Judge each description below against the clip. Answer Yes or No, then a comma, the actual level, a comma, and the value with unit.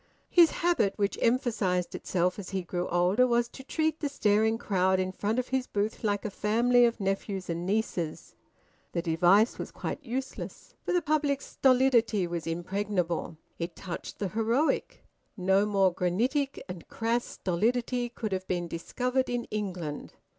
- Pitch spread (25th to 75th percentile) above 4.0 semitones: Yes, average, 5.2 semitones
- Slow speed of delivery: No, average, 160 wpm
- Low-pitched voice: No, high, 210 Hz